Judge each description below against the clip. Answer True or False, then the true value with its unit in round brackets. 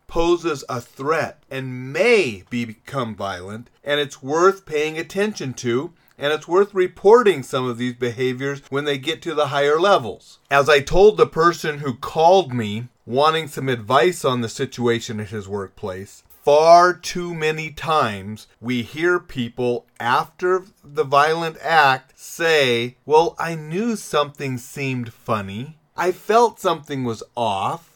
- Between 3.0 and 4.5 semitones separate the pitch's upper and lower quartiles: False (5.3 semitones)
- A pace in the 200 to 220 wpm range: False (150 wpm)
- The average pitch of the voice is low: False (145 Hz)